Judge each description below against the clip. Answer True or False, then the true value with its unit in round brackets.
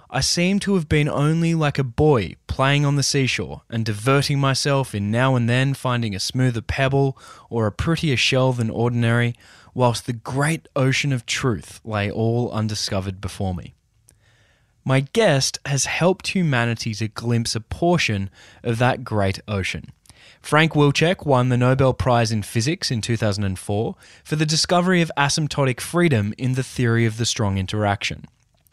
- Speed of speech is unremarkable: True (160 wpm)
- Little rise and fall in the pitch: False (4.4 semitones)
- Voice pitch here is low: True (125 Hz)